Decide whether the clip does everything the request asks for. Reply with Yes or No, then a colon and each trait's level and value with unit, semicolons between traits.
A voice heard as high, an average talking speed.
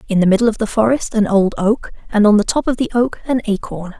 No: high, 220 Hz; fast, 270 wpm